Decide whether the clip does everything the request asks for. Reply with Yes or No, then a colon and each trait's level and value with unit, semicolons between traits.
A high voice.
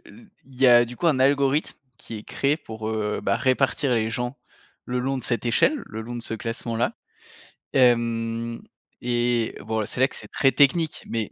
No: low, 120 Hz